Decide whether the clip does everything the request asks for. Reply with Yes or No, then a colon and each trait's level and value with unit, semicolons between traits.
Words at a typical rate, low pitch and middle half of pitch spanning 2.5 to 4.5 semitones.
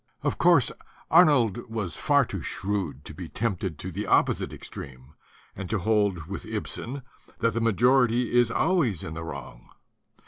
No: average, 160 wpm; low, 105 Hz; average, 5.2 semitones